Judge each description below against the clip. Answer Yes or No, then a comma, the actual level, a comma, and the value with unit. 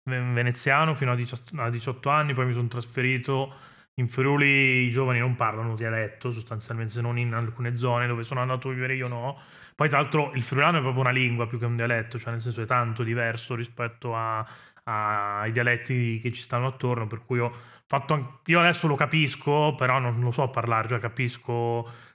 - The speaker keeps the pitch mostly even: Yes, narrow, 2.1 semitones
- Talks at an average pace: No, fast, 200 wpm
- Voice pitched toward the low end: Yes, low, 125 Hz